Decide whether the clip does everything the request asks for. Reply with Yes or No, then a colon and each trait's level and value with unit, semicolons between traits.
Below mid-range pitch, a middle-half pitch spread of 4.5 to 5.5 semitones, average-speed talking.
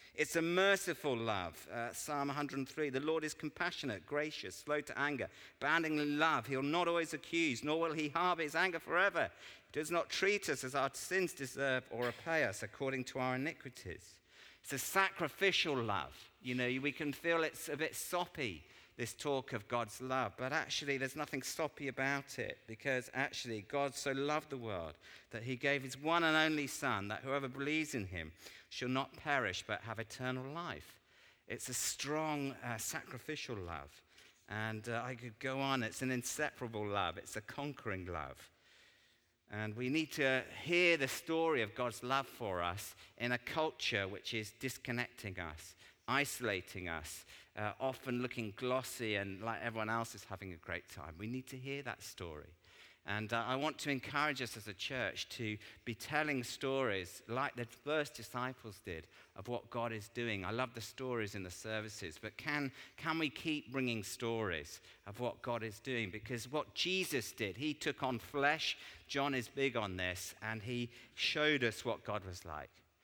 Yes: low, 130 Hz; average, 5.0 semitones; average, 180 wpm